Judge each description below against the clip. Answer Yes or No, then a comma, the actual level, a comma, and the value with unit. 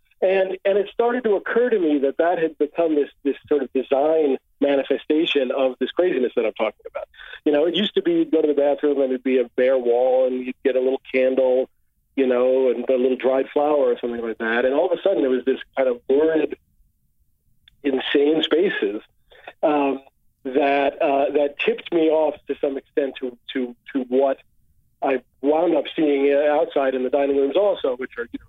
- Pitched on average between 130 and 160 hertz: Yes, medium, 140 Hz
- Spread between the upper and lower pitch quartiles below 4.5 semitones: Yes, average, 4.0 semitones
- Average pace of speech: No, fast, 210 wpm